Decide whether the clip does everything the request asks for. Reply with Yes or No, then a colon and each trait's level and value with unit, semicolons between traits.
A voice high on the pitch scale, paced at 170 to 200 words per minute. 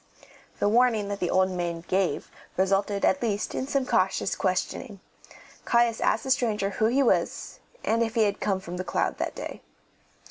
Yes: high, 205 Hz; average, 180 wpm